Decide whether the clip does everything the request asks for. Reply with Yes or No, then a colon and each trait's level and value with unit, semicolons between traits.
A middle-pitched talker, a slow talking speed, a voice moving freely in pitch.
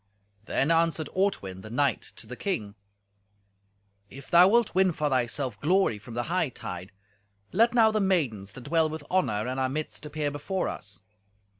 No: medium, 145 Hz; average, 165 wpm; wide, 7.3 semitones